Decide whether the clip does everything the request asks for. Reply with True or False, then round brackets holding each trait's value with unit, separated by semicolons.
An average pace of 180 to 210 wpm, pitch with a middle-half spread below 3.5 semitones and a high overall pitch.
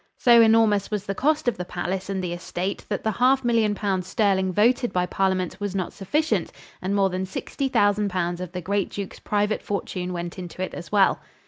True (205 wpm; 2.6 semitones; 195 Hz)